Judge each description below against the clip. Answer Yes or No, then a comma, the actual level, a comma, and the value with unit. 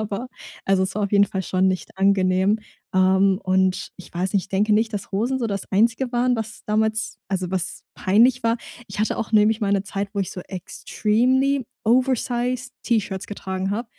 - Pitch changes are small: No, average, 3.2 semitones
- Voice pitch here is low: No, high, 205 Hz